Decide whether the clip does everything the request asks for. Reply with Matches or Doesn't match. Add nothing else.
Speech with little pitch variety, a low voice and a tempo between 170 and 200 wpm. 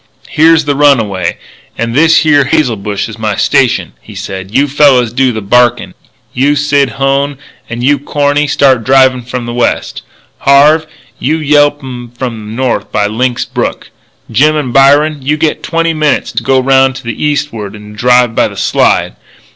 Doesn't match